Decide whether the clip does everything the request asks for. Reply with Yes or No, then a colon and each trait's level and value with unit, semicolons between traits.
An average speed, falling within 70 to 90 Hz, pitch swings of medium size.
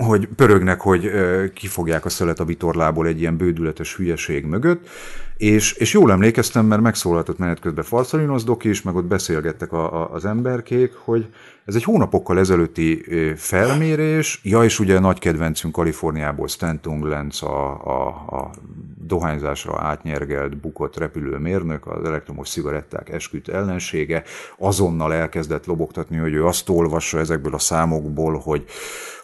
Yes: average, 140 wpm; very low, 85 Hz; average, 4.5 semitones